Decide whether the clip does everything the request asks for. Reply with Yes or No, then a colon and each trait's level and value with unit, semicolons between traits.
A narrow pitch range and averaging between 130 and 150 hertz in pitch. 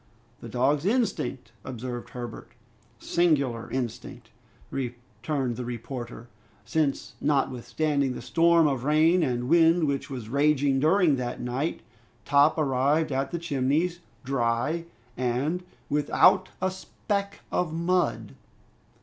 No: average, 4.7 semitones; medium, 140 Hz